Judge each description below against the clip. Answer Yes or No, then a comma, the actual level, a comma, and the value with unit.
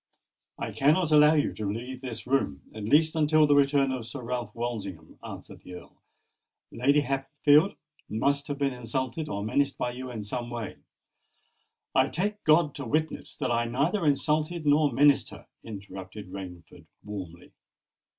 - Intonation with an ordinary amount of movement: Yes, average, 4.7 semitones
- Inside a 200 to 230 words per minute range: No, average, 155 wpm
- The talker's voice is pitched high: No, low, 130 Hz